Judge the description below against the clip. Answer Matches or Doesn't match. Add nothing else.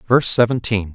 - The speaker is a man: Matches